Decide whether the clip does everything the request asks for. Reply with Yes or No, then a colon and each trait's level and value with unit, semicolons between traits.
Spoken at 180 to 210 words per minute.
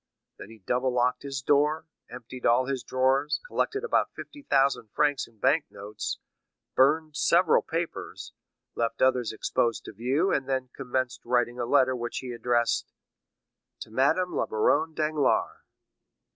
No: average, 145 wpm